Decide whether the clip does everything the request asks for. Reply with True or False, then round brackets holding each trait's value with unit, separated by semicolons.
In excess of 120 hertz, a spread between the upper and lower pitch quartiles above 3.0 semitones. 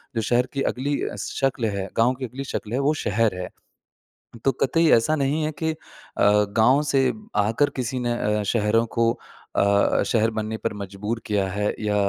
False (115 Hz; 4.3 semitones)